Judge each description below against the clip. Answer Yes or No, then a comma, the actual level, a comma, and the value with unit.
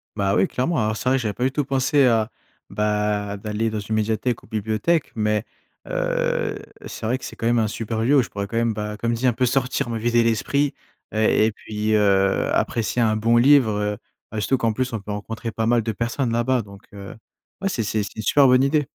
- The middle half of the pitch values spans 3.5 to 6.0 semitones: No, average, 3.1 semitones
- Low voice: Yes, low, 115 Hz